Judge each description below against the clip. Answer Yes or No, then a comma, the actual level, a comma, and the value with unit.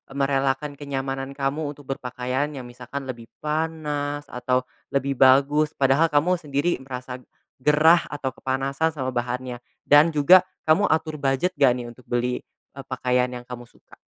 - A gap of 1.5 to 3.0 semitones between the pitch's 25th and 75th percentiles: Yes, average, 2.7 semitones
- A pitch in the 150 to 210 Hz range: No, low, 135 Hz